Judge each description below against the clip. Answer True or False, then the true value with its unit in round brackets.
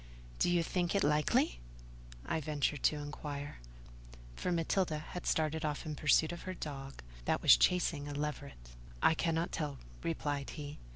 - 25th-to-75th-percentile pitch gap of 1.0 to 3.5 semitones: True (2.4 semitones)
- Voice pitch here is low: False (150 Hz)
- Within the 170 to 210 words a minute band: False (160 wpm)